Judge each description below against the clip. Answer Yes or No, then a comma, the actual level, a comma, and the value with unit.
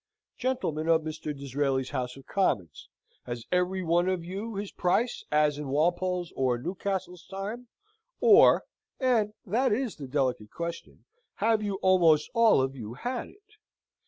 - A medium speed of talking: Yes, average, 150 wpm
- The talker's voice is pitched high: No, medium, 175 Hz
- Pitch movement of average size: No, wide, 6.6 semitones